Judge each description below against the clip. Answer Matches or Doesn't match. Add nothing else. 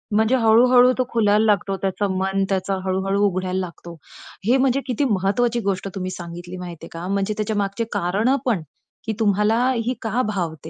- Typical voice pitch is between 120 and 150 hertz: Doesn't match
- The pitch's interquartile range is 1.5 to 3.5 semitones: Matches